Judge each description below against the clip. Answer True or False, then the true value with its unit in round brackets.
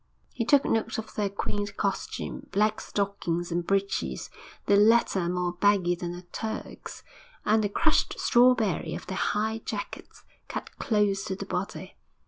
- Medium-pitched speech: False (200 Hz)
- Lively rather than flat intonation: False (3.0 semitones)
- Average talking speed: True (150 wpm)